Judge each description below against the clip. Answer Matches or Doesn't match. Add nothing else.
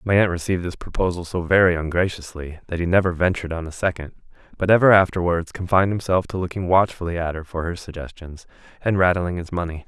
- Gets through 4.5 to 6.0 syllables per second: Doesn't match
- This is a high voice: Doesn't match